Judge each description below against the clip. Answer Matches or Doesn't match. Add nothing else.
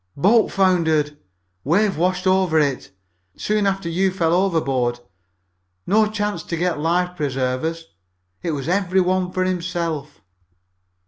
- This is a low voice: Doesn't match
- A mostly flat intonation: Doesn't match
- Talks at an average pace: Doesn't match